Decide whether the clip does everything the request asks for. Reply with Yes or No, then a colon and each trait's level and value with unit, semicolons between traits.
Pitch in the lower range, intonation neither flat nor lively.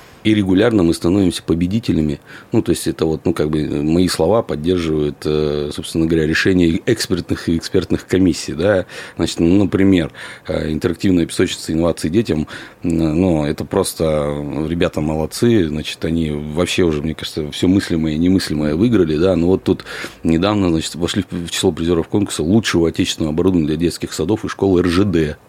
Yes: very low, 85 Hz; average, 3.1 semitones